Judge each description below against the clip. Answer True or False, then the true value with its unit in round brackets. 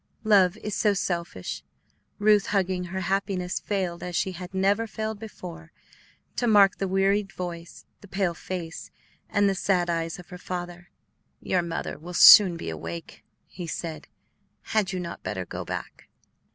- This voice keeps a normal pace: True (160 wpm)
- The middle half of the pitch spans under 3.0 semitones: True (2.5 semitones)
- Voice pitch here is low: False (185 Hz)